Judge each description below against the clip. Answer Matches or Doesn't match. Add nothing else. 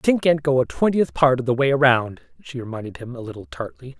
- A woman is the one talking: Doesn't match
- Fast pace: Matches